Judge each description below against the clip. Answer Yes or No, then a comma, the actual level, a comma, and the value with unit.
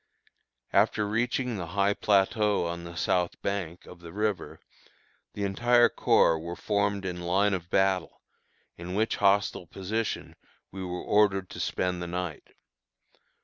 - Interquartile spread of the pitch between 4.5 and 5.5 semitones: No, average, 2.7 semitones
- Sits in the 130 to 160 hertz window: No, very low, 95 Hz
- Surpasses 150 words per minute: No, average, 145 wpm